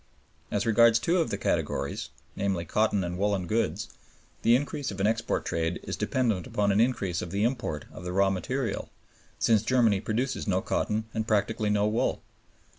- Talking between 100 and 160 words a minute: No, average, 180 wpm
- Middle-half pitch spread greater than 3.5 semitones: No, average, 3.1 semitones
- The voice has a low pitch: Yes, low, 105 Hz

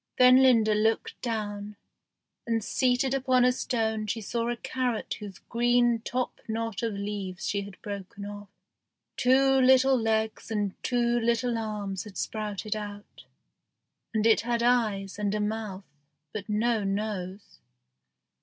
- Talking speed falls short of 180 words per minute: Yes, average, 140 wpm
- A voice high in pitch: Yes, high, 220 Hz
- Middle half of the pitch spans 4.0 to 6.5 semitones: No, average, 2.7 semitones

